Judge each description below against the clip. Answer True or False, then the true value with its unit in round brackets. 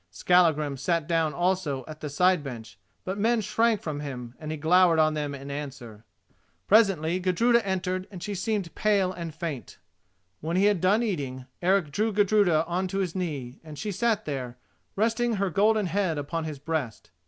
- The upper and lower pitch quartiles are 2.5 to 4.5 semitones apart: False (5.0 semitones)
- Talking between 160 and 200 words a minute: True (180 wpm)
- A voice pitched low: False (175 Hz)